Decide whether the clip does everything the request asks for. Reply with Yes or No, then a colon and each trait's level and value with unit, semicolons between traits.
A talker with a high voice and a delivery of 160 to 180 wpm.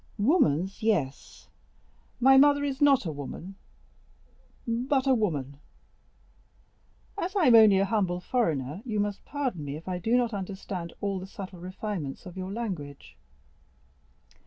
No: high, 200 Hz; slow, 135 wpm